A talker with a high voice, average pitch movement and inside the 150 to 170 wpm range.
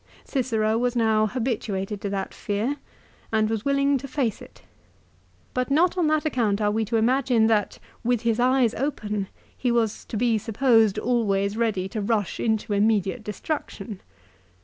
Yes: high, 225 Hz; average, 3.1 semitones; average, 160 wpm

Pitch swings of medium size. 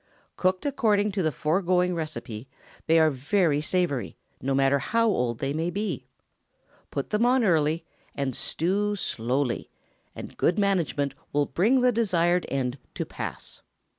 No: wide, 6.2 semitones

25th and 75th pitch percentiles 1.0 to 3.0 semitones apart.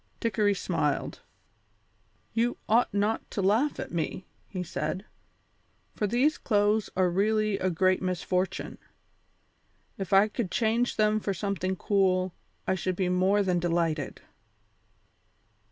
Yes: average, 2.7 semitones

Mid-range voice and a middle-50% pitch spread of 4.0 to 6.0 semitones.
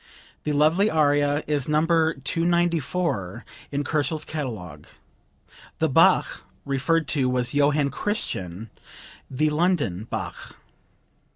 No: medium, 150 Hz; average, 3.5 semitones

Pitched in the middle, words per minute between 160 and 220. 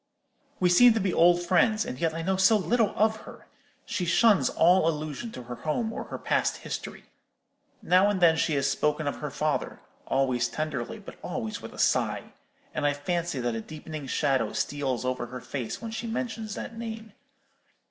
Yes: medium, 165 Hz; average, 190 wpm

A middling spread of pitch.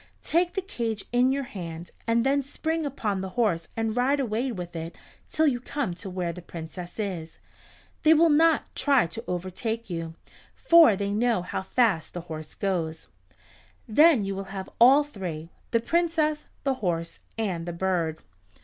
No: wide, 7.6 semitones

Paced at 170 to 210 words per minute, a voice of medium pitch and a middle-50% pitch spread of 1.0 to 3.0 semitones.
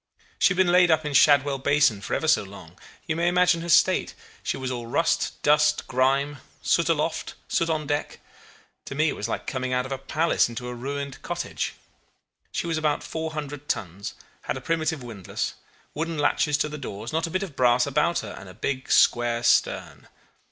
No: average, 200 wpm; medium, 145 Hz; average, 4.0 semitones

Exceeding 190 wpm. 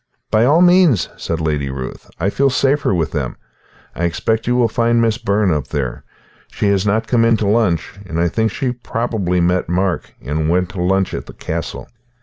Yes: average, 200 wpm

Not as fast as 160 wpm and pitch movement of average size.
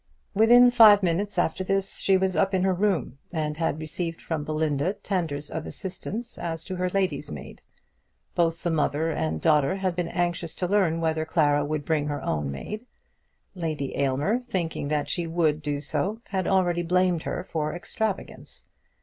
No: average, 175 wpm; average, 3.7 semitones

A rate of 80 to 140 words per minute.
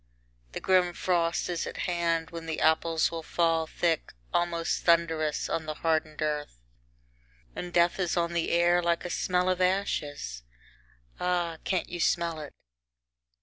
No: average, 150 wpm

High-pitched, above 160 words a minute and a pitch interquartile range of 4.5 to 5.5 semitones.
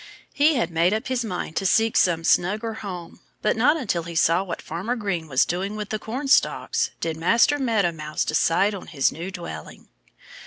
Yes: high, 195 Hz; average, 190 wpm; average, 5.0 semitones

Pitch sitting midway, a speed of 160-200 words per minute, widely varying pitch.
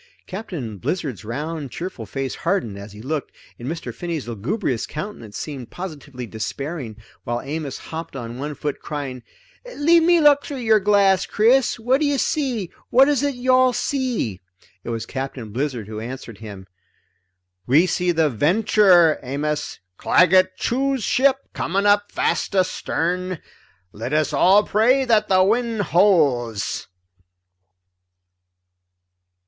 No: medium, 165 Hz; average, 140 wpm; wide, 8.6 semitones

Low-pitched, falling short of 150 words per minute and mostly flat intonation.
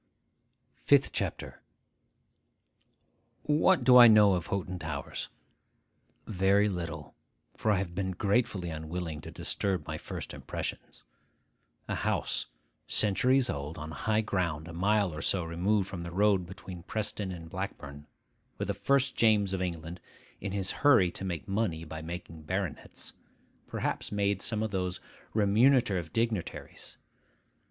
No: very low, 95 Hz; slow, 135 wpm; average, 3.9 semitones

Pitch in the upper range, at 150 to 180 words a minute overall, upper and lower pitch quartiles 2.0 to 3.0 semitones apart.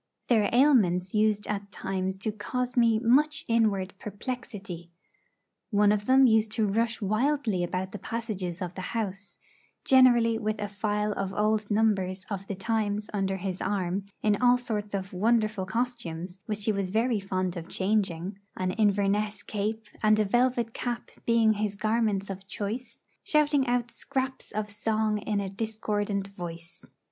Yes: high, 210 Hz; average, 155 wpm; average, 2.7 semitones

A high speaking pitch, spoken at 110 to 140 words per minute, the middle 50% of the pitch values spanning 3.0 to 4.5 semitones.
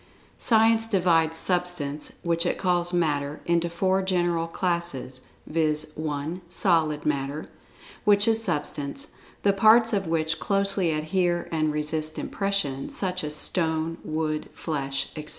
No: medium, 165 Hz; slow, 135 wpm; average, 3.5 semitones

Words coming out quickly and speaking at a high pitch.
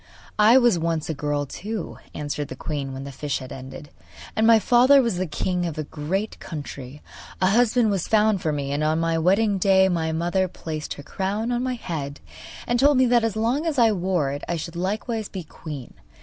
No: fast, 215 wpm; medium, 180 Hz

